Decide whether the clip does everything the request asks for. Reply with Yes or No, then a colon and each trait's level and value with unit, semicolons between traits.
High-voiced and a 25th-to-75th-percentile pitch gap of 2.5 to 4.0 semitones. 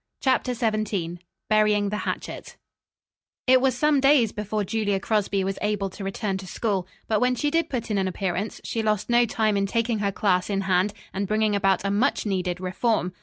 Yes: high, 210 Hz; average, 2.9 semitones